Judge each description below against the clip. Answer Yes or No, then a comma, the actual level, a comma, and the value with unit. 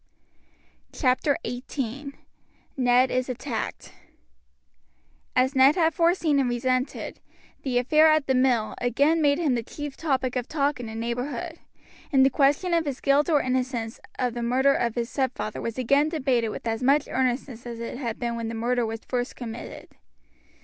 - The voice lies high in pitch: Yes, very high, 255 Hz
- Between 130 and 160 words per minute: No, average, 170 wpm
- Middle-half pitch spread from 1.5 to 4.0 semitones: Yes, average, 2.9 semitones